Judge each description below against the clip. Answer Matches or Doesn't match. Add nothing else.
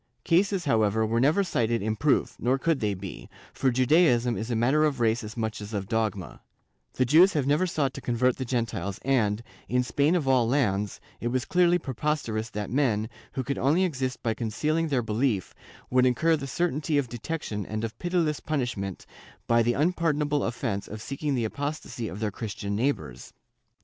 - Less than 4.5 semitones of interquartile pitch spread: Doesn't match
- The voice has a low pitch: Matches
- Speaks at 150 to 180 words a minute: Doesn't match